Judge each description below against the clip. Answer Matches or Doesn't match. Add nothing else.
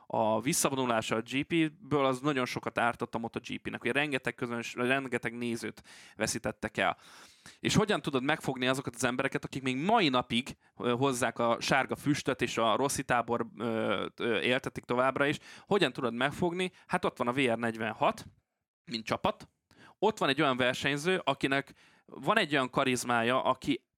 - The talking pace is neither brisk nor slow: Doesn't match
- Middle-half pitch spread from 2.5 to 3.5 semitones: Matches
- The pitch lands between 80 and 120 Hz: Doesn't match